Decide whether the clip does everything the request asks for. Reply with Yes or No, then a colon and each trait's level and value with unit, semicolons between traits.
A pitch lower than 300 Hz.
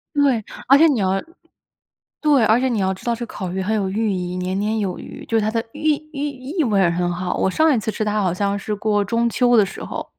Yes: high, 215 Hz